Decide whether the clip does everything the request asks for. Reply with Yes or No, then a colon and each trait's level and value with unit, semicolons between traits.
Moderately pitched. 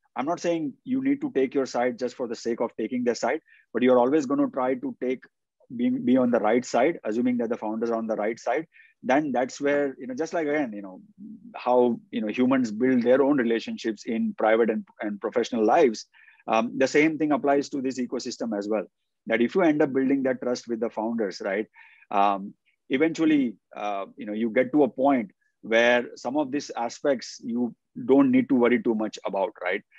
No: low, 130 Hz